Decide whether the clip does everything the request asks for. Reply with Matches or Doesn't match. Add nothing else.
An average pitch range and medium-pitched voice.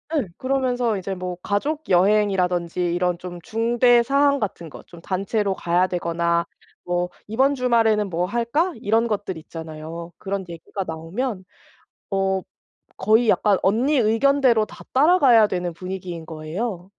Doesn't match